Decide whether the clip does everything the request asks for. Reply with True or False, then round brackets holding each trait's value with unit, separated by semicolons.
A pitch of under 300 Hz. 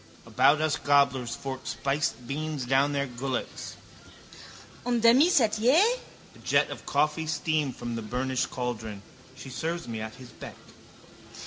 True (140 Hz)